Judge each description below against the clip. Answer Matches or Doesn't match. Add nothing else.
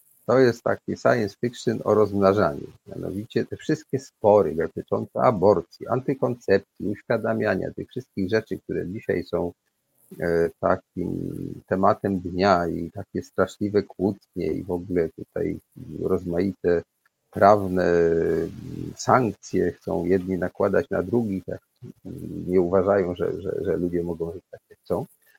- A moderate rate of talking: Matches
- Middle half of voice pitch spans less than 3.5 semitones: Matches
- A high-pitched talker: Doesn't match